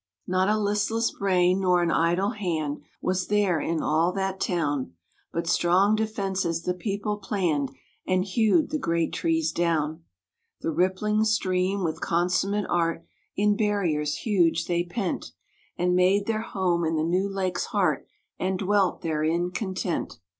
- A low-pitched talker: No, medium, 185 Hz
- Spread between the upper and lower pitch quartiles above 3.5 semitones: No, average, 3.2 semitones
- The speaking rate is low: No, average, 145 wpm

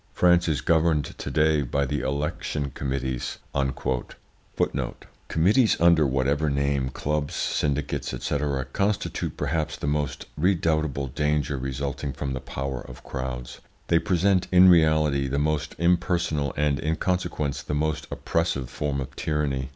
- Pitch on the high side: No, very low, 75 Hz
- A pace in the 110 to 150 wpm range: Yes, slow, 135 wpm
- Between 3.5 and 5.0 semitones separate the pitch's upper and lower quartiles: No, average, 2.8 semitones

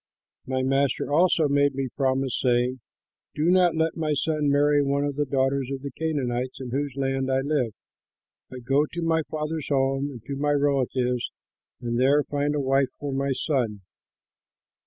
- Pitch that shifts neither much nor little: No, narrow, 1.9 semitones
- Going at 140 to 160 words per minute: No, average, 175 wpm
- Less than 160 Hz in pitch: Yes, medium, 140 Hz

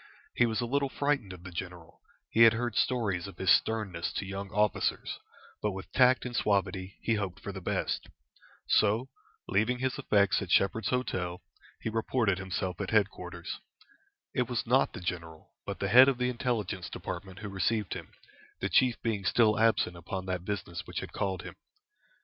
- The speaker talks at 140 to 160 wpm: No, average, 180 wpm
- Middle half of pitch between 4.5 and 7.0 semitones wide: No, average, 3.6 semitones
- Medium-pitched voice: No, low, 100 Hz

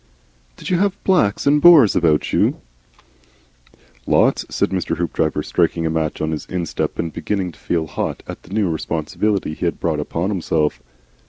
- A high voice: No, very low, 85 Hz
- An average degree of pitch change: Yes, average, 4.7 semitones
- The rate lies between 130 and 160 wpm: No, average, 170 wpm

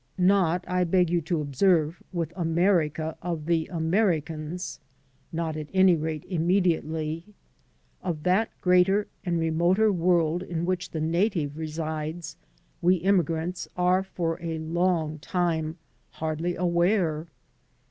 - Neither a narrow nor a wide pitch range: No, narrow, 2.2 semitones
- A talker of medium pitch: Yes, medium, 170 Hz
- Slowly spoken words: Yes, slow, 120 wpm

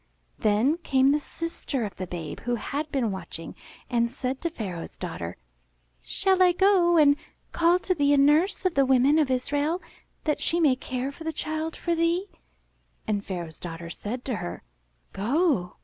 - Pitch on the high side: Yes, very high, 275 Hz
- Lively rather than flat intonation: Yes, wide, 7.4 semitones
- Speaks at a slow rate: No, average, 175 wpm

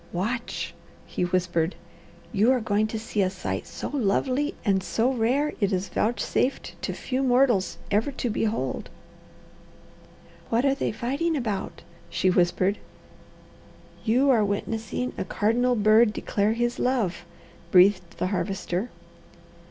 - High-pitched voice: Yes, high, 220 Hz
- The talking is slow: Yes, slow, 130 wpm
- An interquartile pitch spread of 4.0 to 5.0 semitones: Yes, average, 4.5 semitones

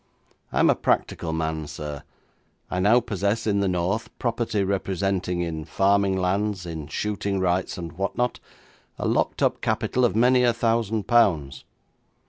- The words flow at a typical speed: Yes, average, 155 wpm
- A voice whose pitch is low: Yes, low, 100 Hz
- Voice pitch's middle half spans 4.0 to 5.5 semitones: Yes, average, 4.3 semitones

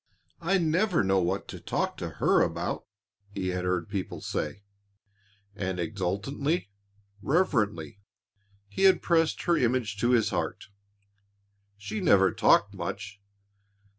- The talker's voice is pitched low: Yes, low, 105 Hz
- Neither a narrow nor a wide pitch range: No, wide, 9.0 semitones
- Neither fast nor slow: No, slow, 125 wpm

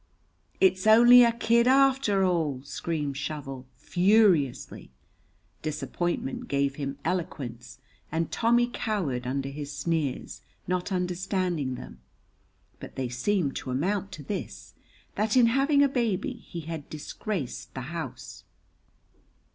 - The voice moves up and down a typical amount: No, wide, 7.4 semitones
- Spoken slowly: Yes, slow, 120 wpm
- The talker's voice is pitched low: No, medium, 175 Hz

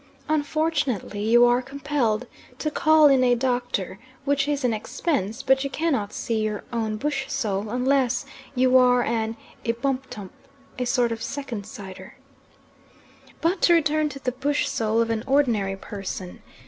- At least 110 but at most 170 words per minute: Yes, average, 150 wpm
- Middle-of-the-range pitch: No, very high, 250 Hz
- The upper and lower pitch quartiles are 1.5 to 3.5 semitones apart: No, average, 4.1 semitones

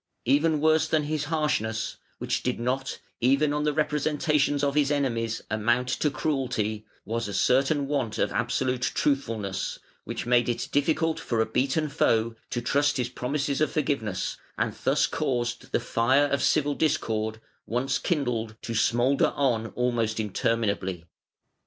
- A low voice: Yes, low, 130 Hz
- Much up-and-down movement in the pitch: No, average, 4.1 semitones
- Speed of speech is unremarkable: Yes, average, 150 wpm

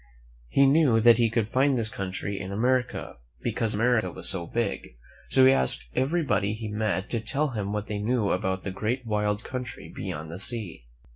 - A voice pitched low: Yes, low, 110 Hz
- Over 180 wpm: Yes, average, 190 wpm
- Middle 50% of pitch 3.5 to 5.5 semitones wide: Yes, average, 3.9 semitones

